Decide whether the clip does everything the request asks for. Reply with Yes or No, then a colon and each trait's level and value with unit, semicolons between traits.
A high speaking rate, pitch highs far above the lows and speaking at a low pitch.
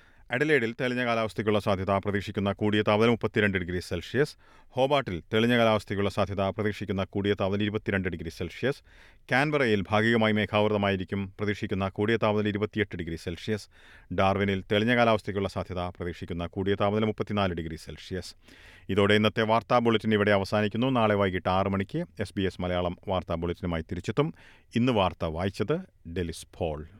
No: fast, 135 wpm; average, 2.9 semitones; low, 100 Hz